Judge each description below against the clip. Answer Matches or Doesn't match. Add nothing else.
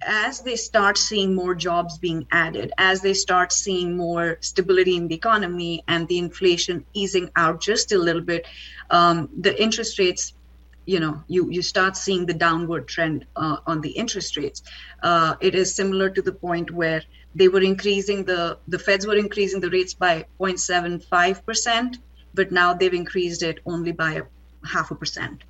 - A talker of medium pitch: Matches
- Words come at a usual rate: Doesn't match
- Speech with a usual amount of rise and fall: Doesn't match